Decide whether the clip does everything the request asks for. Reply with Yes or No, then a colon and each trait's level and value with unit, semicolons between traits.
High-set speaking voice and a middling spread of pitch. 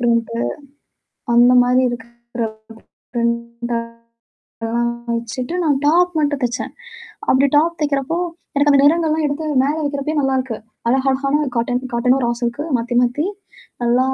Yes: very high, 255 Hz; average, 3.3 semitones